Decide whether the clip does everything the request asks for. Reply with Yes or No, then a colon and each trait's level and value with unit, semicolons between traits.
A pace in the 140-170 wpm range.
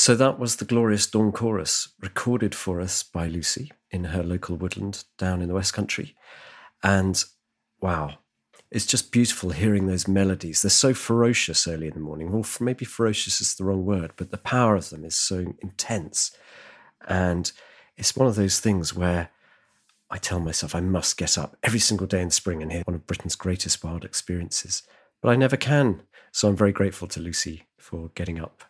No: average, 190 wpm